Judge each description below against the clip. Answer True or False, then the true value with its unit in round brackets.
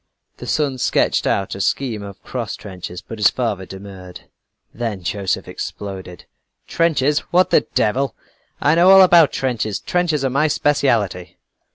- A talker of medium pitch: False (115 Hz)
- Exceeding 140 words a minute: True (150 wpm)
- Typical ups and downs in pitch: False (7.1 semitones)